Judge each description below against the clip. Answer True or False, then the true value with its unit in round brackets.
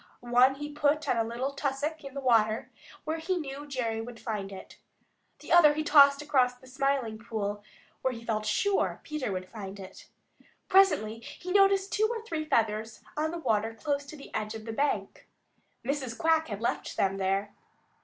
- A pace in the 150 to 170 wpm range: False (185 wpm)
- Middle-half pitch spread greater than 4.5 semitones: True (5.5 semitones)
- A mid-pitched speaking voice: False (260 Hz)